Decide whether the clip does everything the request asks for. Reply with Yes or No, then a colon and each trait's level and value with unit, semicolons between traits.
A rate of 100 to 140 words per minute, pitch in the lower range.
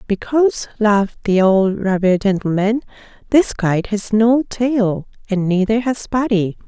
No: slow, 135 wpm; high, 215 Hz